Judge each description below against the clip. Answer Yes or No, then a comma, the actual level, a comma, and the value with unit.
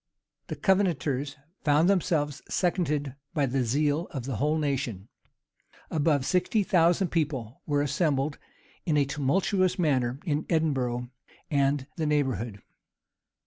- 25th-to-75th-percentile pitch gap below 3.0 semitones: No, average, 3.5 semitones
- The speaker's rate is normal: No, slow, 120 wpm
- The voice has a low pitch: No, medium, 145 Hz